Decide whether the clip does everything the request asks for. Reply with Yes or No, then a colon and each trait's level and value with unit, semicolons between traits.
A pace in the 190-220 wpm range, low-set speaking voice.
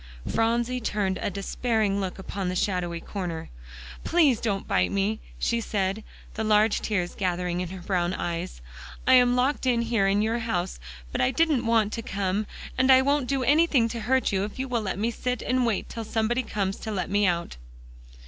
No: average, 195 wpm; high, 215 Hz